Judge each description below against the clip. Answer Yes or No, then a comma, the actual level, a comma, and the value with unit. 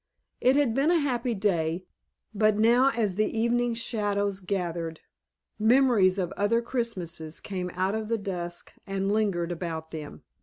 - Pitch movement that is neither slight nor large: Yes, average, 4.5 semitones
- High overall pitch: Yes, high, 205 Hz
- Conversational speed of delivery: Yes, average, 150 wpm